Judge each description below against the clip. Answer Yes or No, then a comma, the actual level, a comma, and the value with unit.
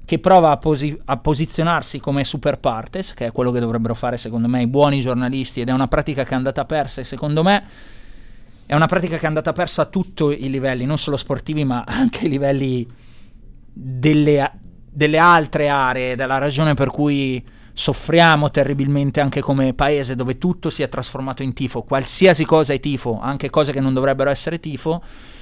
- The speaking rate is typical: No, fast, 190 wpm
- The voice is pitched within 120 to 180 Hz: Yes, medium, 140 Hz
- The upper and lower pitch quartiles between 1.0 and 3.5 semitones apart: Yes, average, 3.0 semitones